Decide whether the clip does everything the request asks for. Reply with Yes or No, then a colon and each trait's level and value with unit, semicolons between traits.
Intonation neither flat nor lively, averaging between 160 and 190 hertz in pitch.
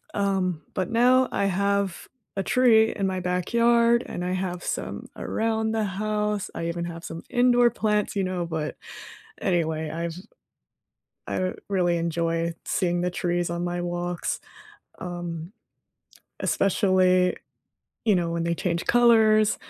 Yes: average, 3.6 semitones; medium, 185 Hz